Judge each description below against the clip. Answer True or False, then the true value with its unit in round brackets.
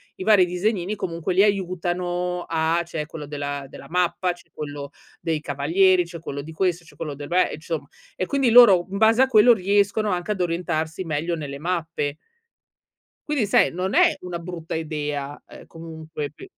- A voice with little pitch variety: False (3.2 semitones)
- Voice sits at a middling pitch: True (175 Hz)